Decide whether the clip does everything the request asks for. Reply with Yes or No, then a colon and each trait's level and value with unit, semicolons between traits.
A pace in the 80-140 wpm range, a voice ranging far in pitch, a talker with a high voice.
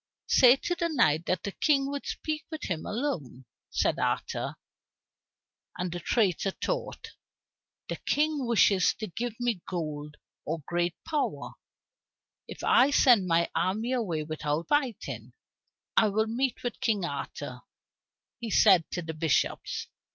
Yes: slow, 135 wpm; wide, 7.4 semitones; high, 205 Hz